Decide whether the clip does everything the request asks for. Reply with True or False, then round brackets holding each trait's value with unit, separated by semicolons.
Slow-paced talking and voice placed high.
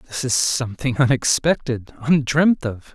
False (120 wpm; 130 Hz)